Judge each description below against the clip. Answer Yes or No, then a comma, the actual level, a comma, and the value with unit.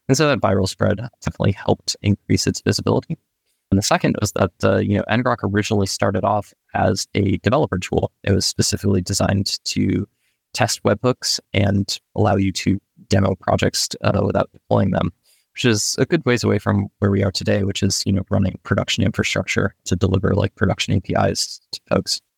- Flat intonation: Yes, narrow, 2.3 semitones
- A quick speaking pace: No, average, 180 wpm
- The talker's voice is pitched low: Yes, low, 100 Hz